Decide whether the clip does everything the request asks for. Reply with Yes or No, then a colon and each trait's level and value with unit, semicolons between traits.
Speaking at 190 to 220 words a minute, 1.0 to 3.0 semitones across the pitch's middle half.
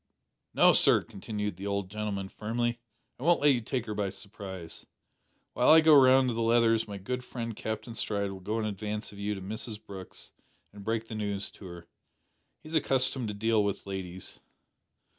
Yes: average, 195 wpm; average, 2.7 semitones